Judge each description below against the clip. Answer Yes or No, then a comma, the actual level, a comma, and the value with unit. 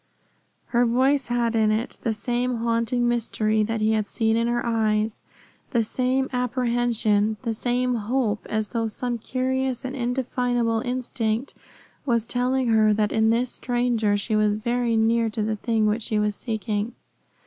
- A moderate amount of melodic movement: No, narrow, 2.1 semitones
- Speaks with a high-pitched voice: Yes, high, 230 Hz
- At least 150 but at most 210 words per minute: Yes, average, 160 wpm